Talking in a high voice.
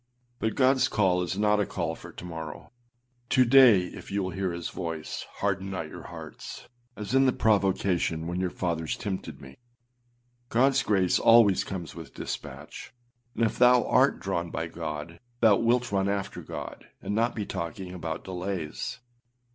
No: low, 100 Hz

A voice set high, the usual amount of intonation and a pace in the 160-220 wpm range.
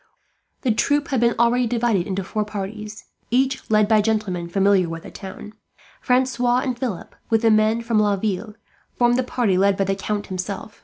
Yes: high, 215 Hz; average, 3.3 semitones; average, 185 wpm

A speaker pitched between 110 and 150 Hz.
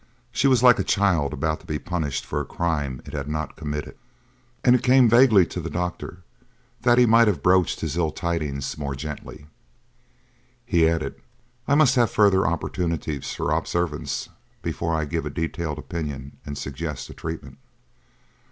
No: very low, 80 Hz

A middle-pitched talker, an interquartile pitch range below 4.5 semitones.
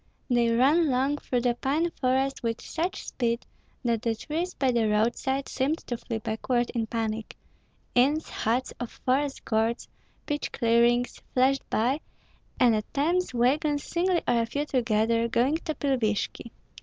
No: very high, 250 Hz; average, 3.5 semitones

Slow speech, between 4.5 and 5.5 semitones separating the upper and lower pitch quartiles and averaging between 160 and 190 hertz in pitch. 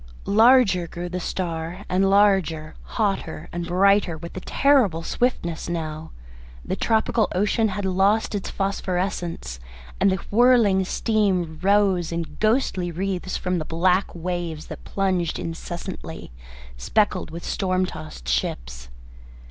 No: slow, 125 wpm; average, 3.2 semitones; medium, 185 Hz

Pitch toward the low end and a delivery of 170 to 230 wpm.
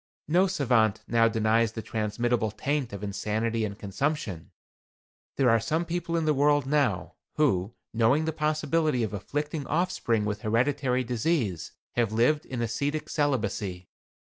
No: low, 120 Hz; average, 145 wpm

